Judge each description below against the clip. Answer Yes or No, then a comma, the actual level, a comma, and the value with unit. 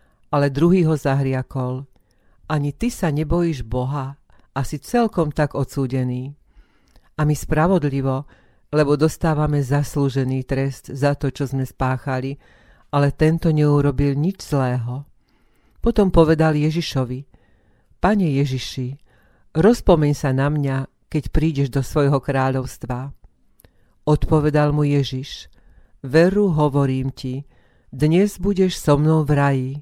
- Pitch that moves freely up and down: No, average, 2.9 semitones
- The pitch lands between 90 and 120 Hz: No, medium, 140 Hz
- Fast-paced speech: No, average, 115 wpm